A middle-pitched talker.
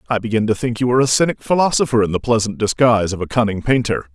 No: low, 115 Hz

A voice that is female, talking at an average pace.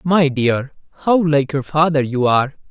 No: male; average, 175 wpm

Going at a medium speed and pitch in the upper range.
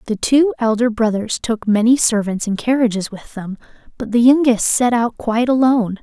Yes: average, 180 wpm; high, 230 Hz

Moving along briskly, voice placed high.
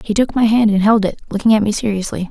Yes: fast, 285 wpm; high, 215 Hz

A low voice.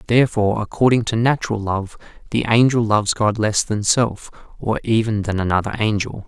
Yes: low, 110 Hz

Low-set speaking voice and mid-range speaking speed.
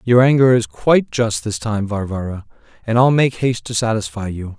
Yes: low, 115 Hz; average, 195 wpm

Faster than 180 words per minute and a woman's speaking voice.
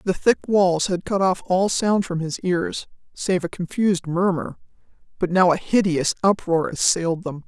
No: average, 175 wpm; female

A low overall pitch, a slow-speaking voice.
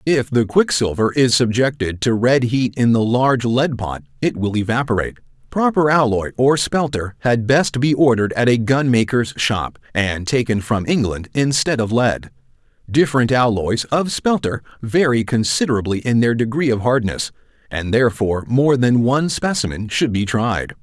No: low, 120 Hz; average, 160 wpm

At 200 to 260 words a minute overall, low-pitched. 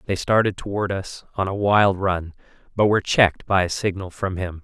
Yes: fast, 205 wpm; very low, 95 Hz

